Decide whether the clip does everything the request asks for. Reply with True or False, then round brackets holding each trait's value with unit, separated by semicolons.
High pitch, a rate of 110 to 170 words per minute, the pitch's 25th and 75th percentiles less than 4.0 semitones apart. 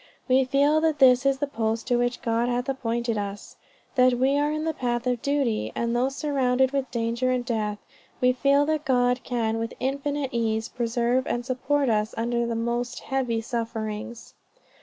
False (245 Hz; 180 wpm; 2.6 semitones)